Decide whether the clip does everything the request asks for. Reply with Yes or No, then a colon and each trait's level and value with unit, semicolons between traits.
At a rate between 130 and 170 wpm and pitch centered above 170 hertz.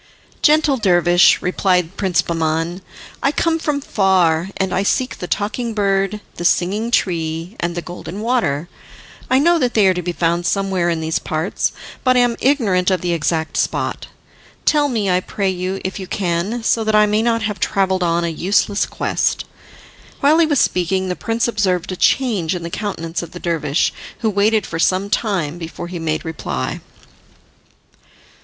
No: average, 180 wpm; high, 190 Hz